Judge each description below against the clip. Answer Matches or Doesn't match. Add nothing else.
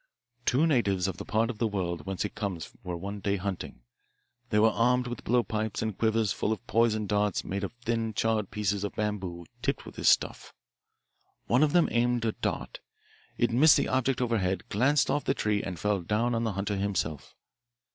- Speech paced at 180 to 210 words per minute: Matches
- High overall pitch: Doesn't match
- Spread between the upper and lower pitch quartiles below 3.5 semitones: Matches